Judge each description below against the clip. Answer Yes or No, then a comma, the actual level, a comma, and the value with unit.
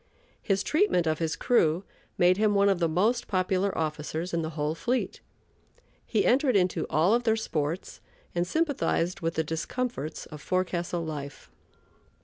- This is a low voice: No, medium, 180 Hz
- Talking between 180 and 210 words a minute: No, average, 155 wpm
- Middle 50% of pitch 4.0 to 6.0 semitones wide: Yes, average, 4.7 semitones